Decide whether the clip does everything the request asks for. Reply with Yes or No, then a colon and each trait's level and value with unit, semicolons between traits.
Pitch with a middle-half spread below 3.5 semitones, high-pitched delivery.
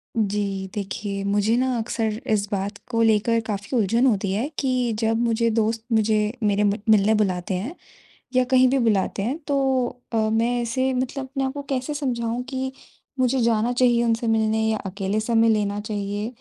Yes: average, 3.0 semitones; high, 225 Hz